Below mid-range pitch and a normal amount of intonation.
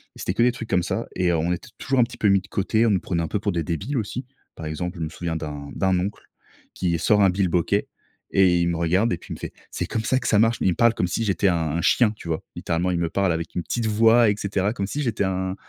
Yes: very low, 95 Hz; average, 4.1 semitones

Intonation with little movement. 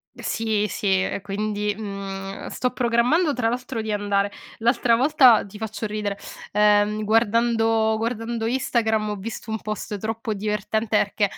Yes: narrow, 2.0 semitones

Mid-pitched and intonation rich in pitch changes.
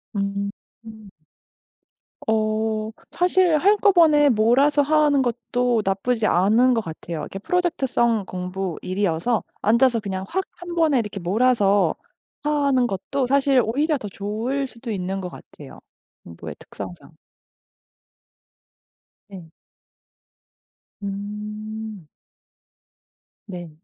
No: high, 220 Hz; wide, 5.7 semitones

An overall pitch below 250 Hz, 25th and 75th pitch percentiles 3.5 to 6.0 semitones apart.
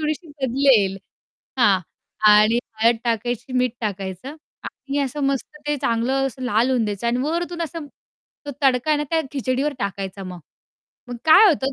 No: very high, 255 Hz; average, 4.5 semitones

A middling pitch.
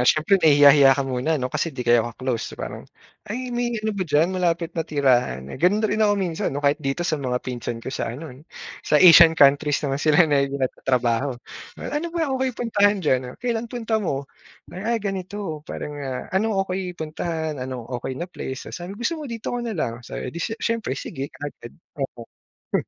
Yes: medium, 160 Hz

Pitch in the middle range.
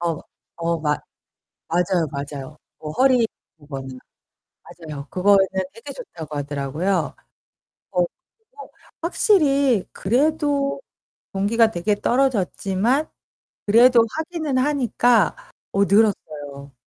No: high, 200 Hz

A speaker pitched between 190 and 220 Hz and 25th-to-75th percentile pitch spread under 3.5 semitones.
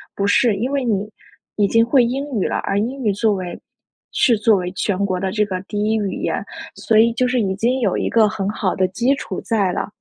Yes: high, 215 Hz; average, 3.0 semitones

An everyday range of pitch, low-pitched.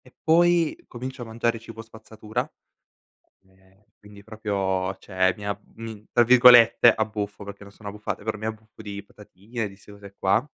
No: narrow, 2.1 semitones; low, 105 Hz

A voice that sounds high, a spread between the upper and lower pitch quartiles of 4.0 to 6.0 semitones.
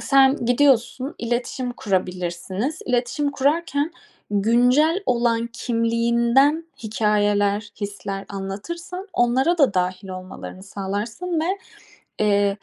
Yes: high, 235 Hz; average, 5.2 semitones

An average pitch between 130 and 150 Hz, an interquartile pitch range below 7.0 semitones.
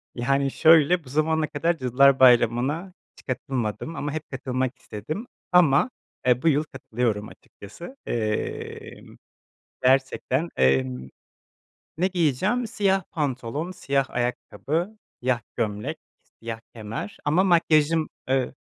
Yes: medium, 140 Hz; average, 5.3 semitones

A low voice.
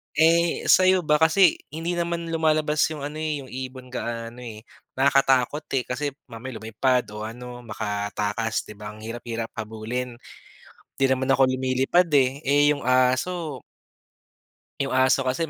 Yes: low, 130 Hz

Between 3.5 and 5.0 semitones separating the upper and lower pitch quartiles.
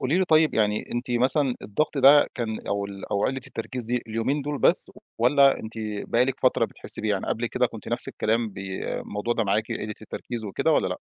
Yes: average, 3.8 semitones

